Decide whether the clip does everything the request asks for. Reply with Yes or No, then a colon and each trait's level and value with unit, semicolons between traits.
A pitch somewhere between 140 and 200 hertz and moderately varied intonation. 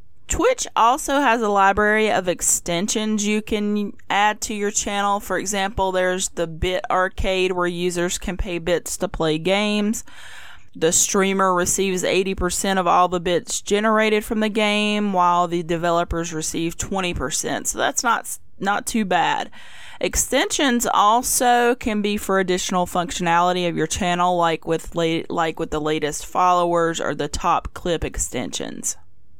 Yes: medium, 185 Hz; average, 3.2 semitones